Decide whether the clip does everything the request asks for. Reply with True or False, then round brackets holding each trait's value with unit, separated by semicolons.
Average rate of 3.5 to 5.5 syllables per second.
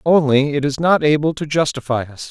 True (5.4 syllables/s)